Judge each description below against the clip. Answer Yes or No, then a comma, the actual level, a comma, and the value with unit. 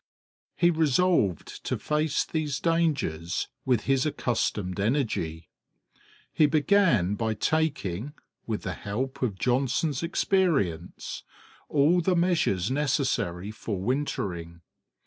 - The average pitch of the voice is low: Yes, low, 130 Hz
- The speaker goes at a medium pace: No, slow, 105 wpm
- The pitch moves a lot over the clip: Yes, wide, 7.9 semitones